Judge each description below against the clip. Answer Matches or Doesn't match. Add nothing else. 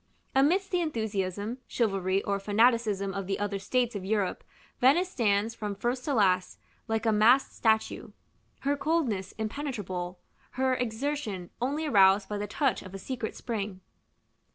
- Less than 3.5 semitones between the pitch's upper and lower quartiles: Doesn't match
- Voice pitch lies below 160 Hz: Doesn't match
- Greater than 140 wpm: Matches